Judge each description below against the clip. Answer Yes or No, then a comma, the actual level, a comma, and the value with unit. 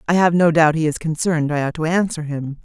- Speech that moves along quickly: Yes, fast, 275 wpm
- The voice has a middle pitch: Yes, medium, 160 Hz